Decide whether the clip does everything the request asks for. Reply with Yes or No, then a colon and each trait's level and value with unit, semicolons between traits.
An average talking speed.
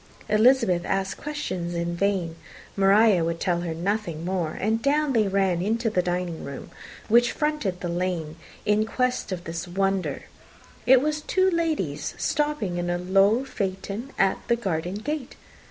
Yes: average, 155 wpm